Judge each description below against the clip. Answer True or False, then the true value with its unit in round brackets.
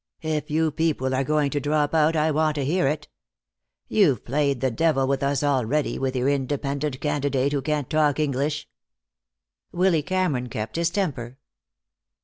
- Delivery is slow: False (160 wpm)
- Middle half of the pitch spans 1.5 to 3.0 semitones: True (2.4 semitones)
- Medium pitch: True (145 Hz)